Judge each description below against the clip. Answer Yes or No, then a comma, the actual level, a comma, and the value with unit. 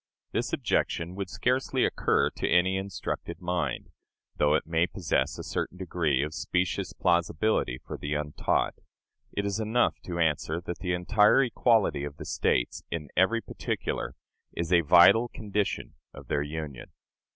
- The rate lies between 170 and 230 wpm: No, average, 150 wpm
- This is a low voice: Yes, very low, 90 Hz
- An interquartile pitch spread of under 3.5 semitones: No, average, 4.4 semitones